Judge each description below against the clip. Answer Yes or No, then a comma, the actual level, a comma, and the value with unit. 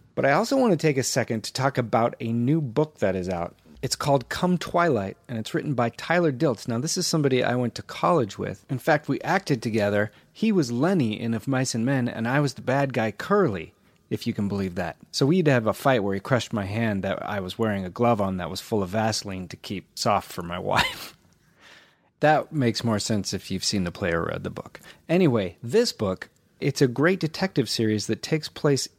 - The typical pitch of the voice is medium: No, low, 120 Hz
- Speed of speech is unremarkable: No, fast, 230 wpm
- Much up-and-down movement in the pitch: Yes, wide, 6.1 semitones